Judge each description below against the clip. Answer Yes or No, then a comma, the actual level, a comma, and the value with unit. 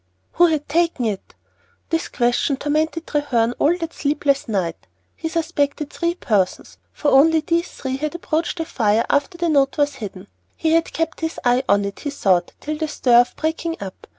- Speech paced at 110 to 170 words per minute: No, average, 180 wpm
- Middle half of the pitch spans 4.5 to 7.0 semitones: Yes, average, 5.0 semitones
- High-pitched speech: Yes, very high, 290 Hz